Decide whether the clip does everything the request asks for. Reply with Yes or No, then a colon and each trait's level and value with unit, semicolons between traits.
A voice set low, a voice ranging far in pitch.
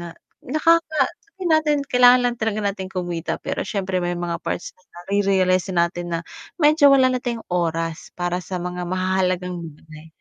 No: medium, 185 Hz; wide, 6.1 semitones